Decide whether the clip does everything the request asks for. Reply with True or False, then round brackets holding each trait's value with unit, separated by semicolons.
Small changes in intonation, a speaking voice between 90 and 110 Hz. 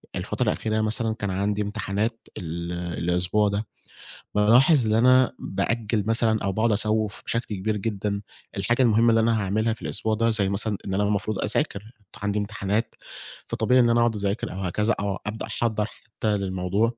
True (2.2 semitones; 105 Hz)